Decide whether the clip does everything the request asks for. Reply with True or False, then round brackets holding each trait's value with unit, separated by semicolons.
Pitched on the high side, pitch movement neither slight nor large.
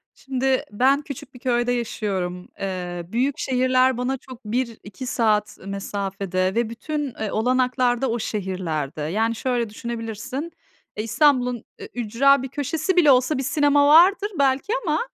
True (245 Hz; 4.2 semitones)